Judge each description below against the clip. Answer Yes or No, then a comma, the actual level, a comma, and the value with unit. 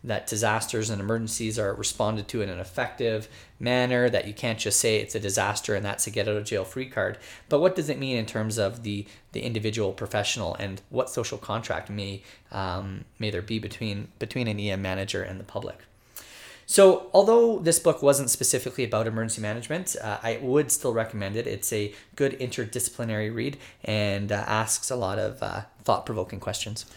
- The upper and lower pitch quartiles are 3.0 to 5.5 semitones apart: Yes, average, 3.3 semitones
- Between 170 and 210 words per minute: Yes, average, 195 wpm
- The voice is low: Yes, low, 110 Hz